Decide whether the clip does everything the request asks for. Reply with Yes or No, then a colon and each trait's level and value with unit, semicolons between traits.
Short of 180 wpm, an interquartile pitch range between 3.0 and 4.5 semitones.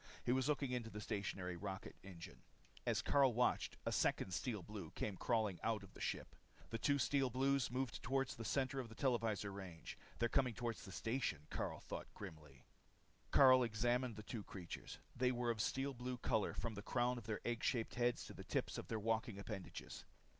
No: average, 200 wpm; average, 3.8 semitones